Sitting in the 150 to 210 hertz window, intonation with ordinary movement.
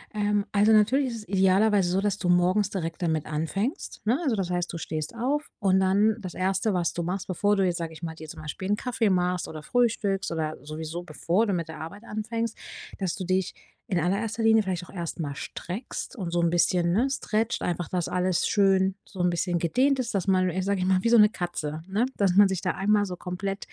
Yes: high, 190 Hz; average, 3.2 semitones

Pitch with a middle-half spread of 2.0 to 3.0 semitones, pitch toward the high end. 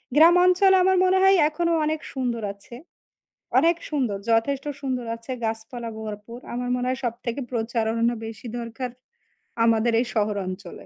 No: average, 3.8 semitones; high, 240 Hz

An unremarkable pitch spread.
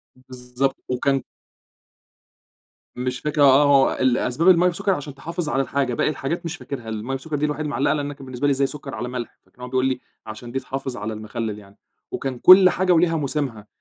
Yes: average, 3.1 semitones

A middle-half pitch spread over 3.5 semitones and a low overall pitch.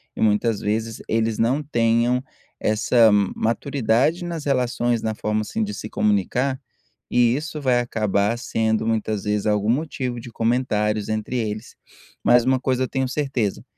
No: average, 3.1 semitones; low, 115 Hz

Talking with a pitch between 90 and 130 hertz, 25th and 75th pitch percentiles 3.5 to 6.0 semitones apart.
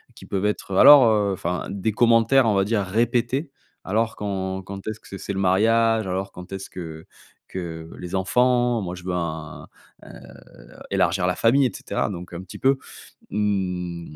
Yes: low, 100 Hz; average, 3.9 semitones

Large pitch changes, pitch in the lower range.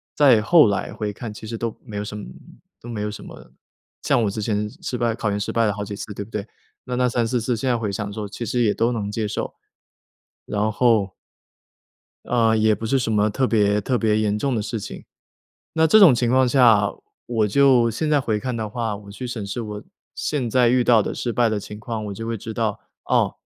No: average, 2.7 semitones; low, 110 Hz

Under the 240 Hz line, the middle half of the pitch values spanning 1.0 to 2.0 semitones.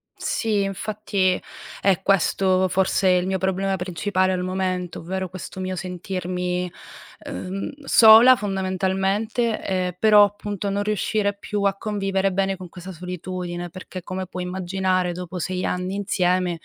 Yes: high, 190 Hz; narrow, 1.4 semitones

